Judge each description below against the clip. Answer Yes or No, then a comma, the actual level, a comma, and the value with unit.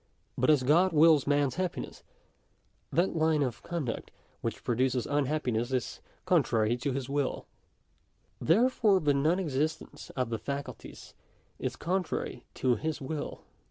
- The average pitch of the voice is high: No, medium, 145 Hz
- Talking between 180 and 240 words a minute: No, slow, 135 wpm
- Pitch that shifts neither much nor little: Yes, average, 3.9 semitones